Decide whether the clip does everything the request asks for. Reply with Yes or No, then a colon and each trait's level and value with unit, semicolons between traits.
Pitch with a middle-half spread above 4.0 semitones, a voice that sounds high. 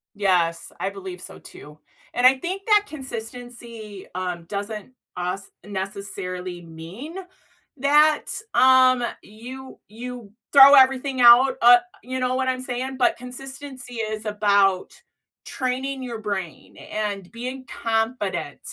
Yes: average, 4.6 semitones; high, 235 Hz